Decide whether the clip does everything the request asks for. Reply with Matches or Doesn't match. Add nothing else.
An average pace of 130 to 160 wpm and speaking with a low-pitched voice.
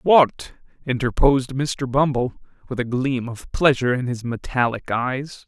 Matches